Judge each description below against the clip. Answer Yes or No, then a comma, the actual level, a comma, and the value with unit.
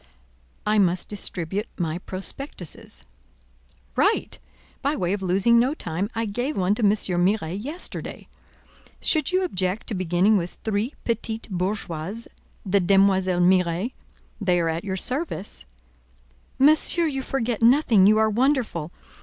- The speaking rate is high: No, slow, 135 wpm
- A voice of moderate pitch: No, high, 200 Hz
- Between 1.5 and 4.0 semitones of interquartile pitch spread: No, average, 4.4 semitones